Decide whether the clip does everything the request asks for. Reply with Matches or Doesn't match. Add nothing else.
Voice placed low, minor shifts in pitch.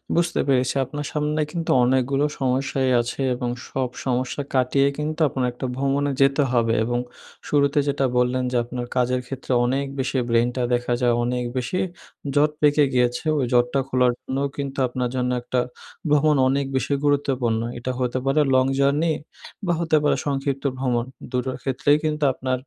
Matches